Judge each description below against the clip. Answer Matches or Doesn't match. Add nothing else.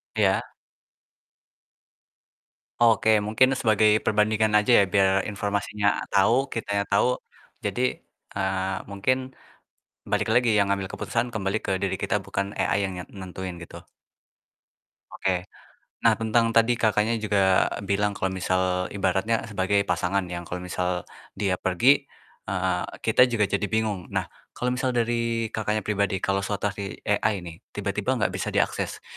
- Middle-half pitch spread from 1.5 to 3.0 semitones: Matches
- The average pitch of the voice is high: Doesn't match